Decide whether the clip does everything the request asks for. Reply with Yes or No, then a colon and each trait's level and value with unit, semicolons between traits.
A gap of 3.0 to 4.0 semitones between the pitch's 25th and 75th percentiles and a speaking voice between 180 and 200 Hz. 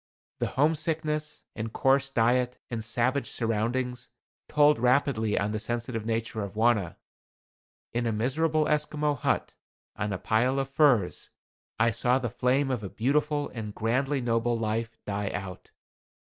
No: average, 3.7 semitones; low, 120 Hz